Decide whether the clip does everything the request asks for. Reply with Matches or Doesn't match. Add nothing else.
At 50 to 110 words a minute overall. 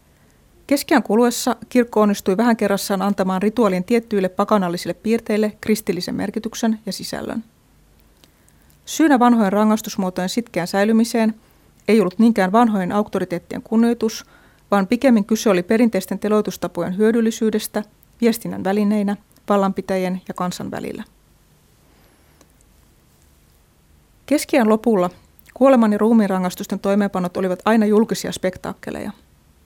Matches